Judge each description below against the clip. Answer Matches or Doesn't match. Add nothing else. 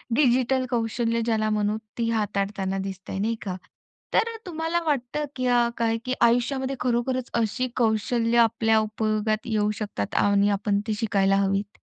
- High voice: Matches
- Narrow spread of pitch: Doesn't match